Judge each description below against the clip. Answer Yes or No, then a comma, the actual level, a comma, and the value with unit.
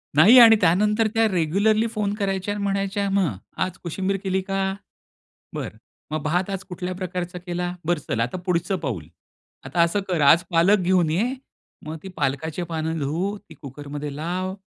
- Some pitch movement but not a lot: Yes, average, 3.5 semitones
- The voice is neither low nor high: Yes, medium, 180 Hz